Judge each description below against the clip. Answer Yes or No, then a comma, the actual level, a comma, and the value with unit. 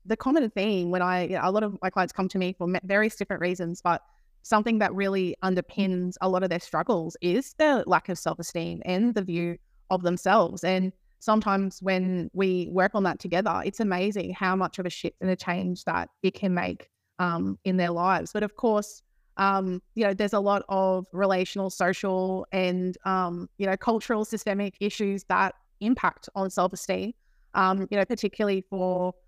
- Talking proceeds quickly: No, average, 195 wpm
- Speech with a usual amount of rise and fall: No, narrow, 1.9 semitones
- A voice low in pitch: No, high, 190 Hz